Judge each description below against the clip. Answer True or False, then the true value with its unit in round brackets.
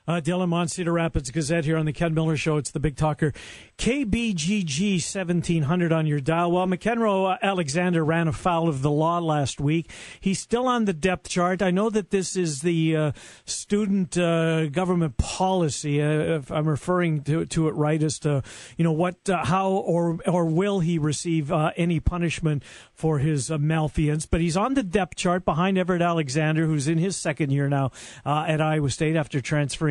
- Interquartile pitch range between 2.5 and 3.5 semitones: True (2.8 semitones)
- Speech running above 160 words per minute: True (195 wpm)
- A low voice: False (165 Hz)